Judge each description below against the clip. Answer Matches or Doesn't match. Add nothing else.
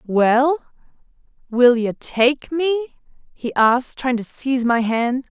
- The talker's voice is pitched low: Doesn't match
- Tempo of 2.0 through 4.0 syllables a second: Matches